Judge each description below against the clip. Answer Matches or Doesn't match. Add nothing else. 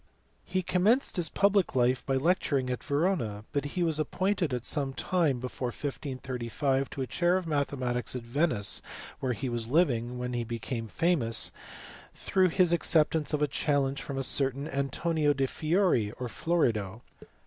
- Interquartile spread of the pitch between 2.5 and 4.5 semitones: Doesn't match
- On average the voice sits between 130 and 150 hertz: Matches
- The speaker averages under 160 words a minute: Doesn't match